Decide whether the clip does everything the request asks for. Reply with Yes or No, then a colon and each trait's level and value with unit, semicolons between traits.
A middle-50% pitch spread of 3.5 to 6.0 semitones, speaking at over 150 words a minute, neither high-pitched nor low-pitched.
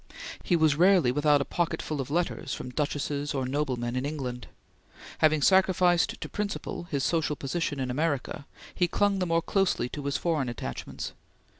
Yes: average, 4.2 semitones; average, 170 wpm; medium, 150 Hz